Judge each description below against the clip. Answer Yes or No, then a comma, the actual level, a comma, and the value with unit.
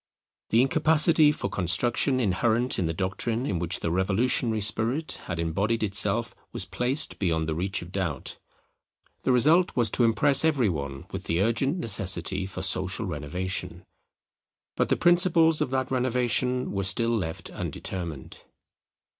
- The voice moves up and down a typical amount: No, wide, 5.7 semitones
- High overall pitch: No, low, 110 Hz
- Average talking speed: Yes, average, 145 wpm